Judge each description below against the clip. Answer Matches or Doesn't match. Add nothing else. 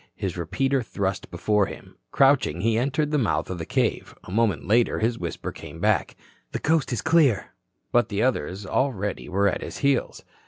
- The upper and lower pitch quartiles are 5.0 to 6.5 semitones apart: Matches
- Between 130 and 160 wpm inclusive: Doesn't match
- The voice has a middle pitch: Doesn't match